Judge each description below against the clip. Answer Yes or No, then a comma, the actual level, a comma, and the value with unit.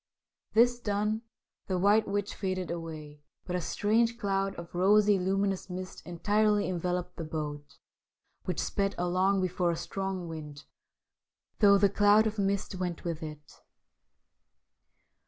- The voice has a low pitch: No, high, 190 Hz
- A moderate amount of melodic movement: Yes, average, 3.0 semitones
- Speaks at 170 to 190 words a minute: No, slow, 135 wpm